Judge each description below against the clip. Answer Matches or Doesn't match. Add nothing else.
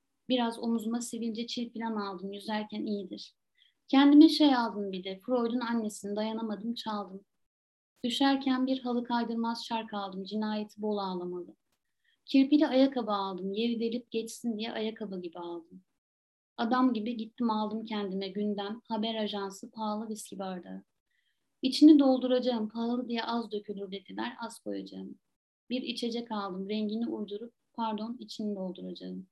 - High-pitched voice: Matches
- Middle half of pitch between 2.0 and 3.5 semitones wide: Matches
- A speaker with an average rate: Matches